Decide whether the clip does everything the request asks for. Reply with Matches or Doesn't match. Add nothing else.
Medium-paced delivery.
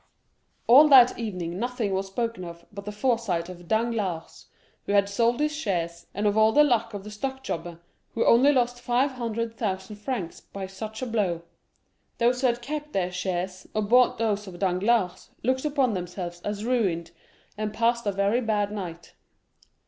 Matches